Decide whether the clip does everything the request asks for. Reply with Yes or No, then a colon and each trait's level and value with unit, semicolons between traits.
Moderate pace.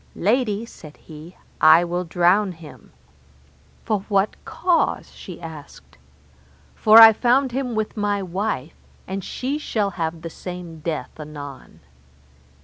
No: slow, 130 wpm